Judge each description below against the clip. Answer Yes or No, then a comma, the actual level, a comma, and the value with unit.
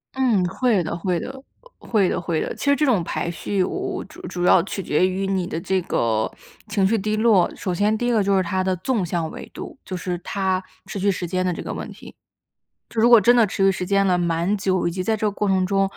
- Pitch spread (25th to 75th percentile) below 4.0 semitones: Yes, average, 2.8 semitones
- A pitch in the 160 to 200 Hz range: Yes, high, 190 Hz